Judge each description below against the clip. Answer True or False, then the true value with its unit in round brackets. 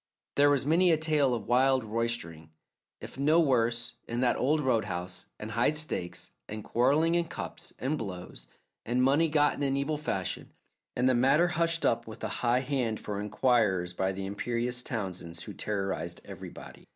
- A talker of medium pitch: False (120 Hz)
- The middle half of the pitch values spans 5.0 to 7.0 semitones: True (5.5 semitones)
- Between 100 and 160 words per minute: False (170 wpm)